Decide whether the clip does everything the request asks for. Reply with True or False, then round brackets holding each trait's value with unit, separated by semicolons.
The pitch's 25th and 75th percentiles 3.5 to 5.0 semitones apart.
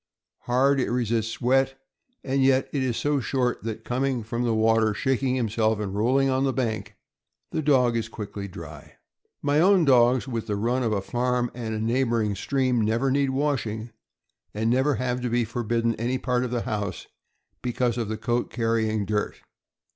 False (2.9 semitones)